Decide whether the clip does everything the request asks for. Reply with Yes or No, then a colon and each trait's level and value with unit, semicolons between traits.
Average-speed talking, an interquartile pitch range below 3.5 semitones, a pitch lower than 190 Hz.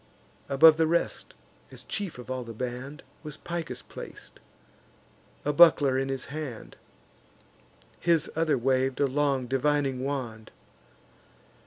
No: slow, 125 wpm; average, 3.0 semitones; medium, 140 Hz